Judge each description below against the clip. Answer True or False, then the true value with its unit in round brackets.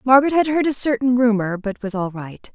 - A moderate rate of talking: False (235 wpm)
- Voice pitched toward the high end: True (235 Hz)